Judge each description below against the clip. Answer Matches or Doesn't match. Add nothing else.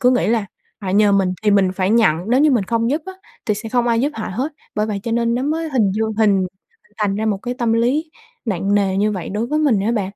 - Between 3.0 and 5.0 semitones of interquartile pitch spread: Matches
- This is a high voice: Matches